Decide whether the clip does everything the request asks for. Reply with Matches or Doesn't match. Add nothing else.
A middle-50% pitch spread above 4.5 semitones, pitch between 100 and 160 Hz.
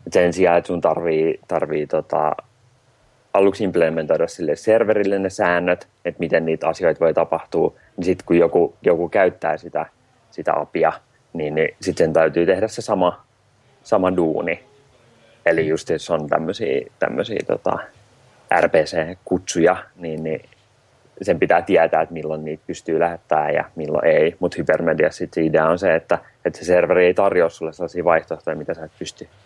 Doesn't match